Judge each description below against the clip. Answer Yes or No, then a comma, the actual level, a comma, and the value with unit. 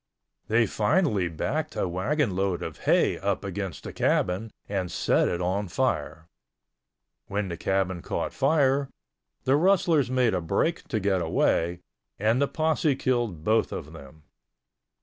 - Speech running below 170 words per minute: Yes, average, 145 wpm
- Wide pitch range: Yes, wide, 7.2 semitones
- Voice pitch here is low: Yes, low, 105 Hz